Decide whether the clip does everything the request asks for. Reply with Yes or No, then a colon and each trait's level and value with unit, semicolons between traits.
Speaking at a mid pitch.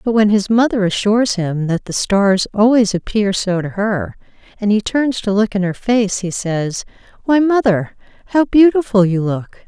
No: high, 210 Hz